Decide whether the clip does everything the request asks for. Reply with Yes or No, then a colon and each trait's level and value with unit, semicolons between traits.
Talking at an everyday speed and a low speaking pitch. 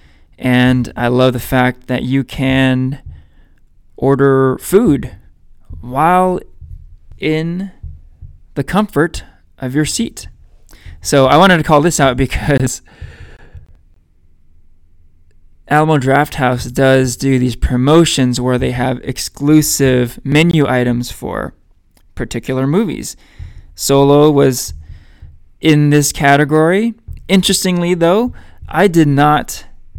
No: slow, 100 wpm; low, 125 Hz